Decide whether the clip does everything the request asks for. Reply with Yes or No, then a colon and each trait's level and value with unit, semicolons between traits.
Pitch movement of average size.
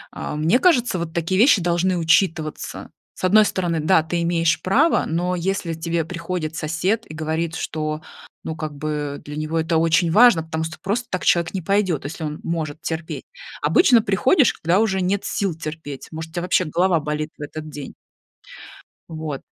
Yes: average, 3.1 semitones